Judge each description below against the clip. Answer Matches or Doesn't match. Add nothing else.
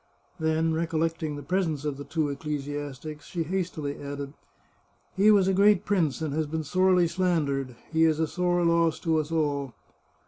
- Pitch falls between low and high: Matches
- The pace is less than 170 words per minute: Doesn't match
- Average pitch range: Matches